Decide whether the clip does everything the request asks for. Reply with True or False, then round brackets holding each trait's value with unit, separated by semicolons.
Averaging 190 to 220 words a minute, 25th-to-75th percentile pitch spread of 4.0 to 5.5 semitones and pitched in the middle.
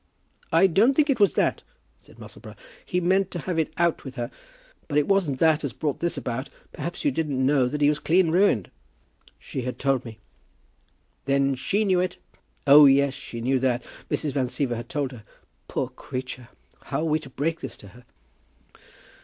True (195 wpm; 4.7 semitones; 145 Hz)